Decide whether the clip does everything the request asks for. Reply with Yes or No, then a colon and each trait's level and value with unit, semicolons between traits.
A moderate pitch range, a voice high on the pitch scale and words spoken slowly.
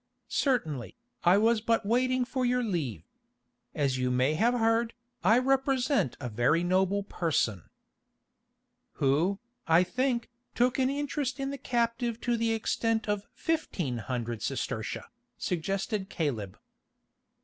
No: wide, 7.9 semitones; high, 220 Hz; slow, 125 wpm